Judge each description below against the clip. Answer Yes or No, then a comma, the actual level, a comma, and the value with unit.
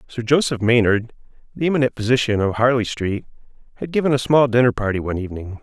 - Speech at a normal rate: Yes, average, 180 wpm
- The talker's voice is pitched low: Yes, low, 120 Hz